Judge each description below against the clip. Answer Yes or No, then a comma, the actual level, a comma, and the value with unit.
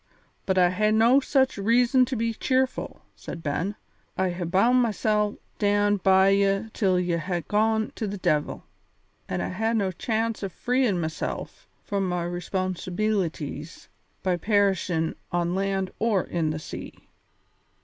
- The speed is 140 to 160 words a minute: Yes, average, 150 wpm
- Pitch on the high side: Yes, high, 195 Hz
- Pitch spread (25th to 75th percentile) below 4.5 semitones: Yes, average, 3.6 semitones